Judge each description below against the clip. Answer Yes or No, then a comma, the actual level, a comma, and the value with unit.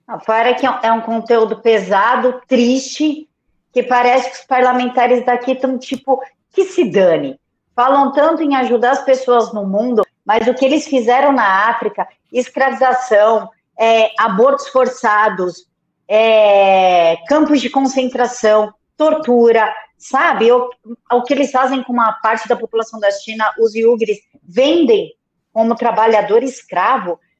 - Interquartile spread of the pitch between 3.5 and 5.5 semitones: No, average, 3.1 semitones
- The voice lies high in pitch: Yes, high, 245 Hz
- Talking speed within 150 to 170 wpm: No, average, 135 wpm